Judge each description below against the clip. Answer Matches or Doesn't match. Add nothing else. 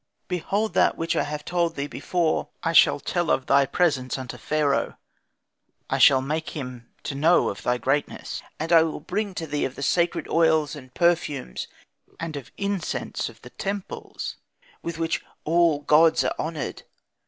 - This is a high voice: Doesn't match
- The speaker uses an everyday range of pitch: Matches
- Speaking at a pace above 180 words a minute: Doesn't match